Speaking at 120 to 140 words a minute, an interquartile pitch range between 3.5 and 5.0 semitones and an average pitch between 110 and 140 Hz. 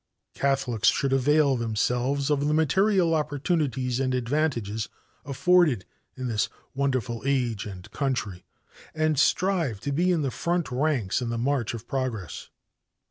Yes: slow, 135 wpm; average, 4.4 semitones; low, 135 Hz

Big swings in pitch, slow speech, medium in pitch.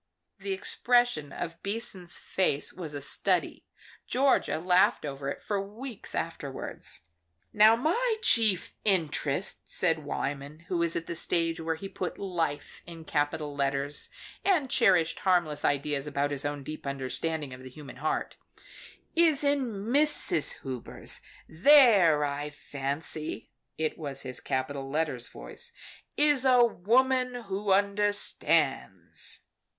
Yes: wide, 6.9 semitones; slow, 130 wpm; medium, 165 Hz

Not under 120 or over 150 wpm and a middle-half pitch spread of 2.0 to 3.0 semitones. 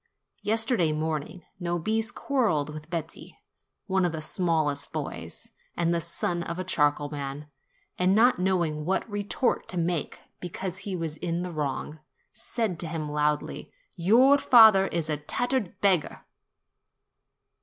No: average, 140 wpm; average, 4.2 semitones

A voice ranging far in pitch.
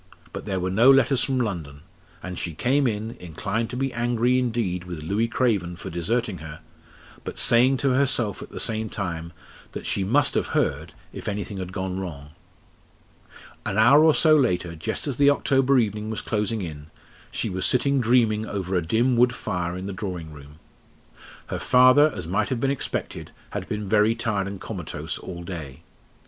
Yes: wide, 5.8 semitones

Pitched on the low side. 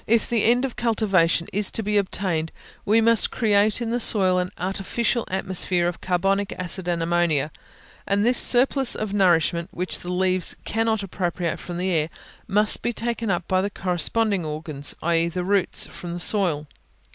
No: high, 190 Hz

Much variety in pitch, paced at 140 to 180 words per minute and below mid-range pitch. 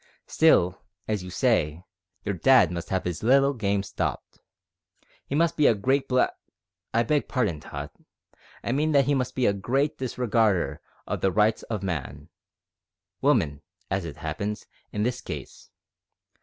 Yes: wide, 6.6 semitones; average, 155 wpm; low, 105 Hz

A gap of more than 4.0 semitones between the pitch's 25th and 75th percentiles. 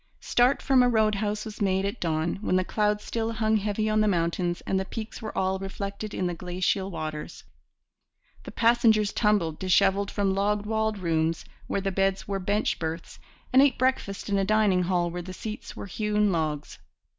No: average, 2.8 semitones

